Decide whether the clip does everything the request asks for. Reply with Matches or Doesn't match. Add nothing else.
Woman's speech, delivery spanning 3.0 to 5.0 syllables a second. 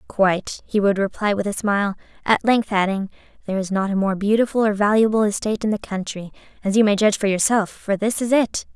Doesn't match